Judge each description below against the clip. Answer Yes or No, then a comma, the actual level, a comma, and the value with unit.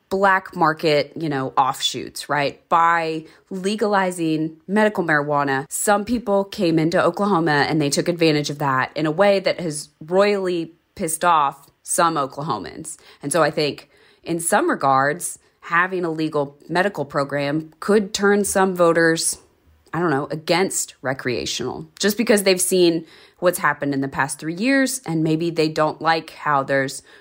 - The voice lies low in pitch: No, medium, 165 Hz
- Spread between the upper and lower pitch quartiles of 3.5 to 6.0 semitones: Yes, average, 4.2 semitones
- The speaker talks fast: No, average, 155 wpm